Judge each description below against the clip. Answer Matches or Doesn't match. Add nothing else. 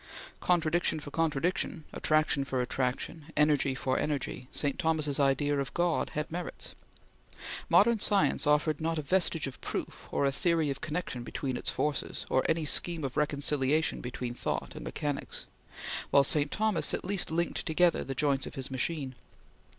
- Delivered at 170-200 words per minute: Doesn't match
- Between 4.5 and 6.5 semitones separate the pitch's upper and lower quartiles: Doesn't match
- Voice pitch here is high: Doesn't match